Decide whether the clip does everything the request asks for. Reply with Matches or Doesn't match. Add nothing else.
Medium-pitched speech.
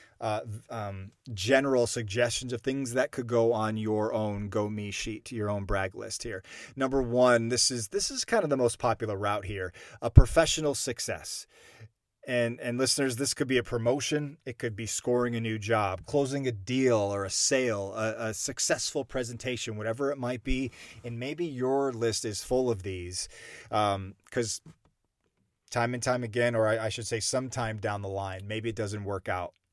Doesn't match